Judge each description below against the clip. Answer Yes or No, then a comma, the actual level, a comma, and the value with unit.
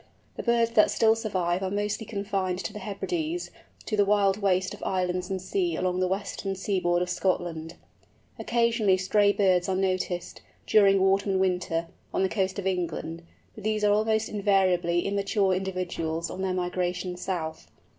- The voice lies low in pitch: No, high, 190 Hz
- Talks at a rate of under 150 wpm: No, average, 165 wpm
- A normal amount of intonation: No, narrow, 2.3 semitones